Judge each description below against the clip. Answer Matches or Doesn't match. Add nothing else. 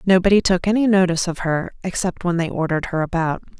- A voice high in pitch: Doesn't match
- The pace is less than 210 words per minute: Matches